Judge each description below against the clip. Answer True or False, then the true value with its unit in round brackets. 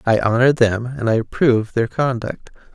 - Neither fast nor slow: True (175 wpm)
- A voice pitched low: True (120 Hz)